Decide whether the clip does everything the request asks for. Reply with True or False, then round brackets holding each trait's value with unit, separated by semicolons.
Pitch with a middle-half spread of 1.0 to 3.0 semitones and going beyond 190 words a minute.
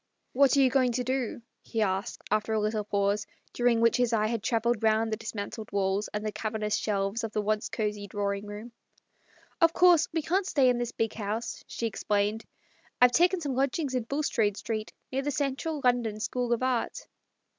False (3.4 semitones; 200 wpm)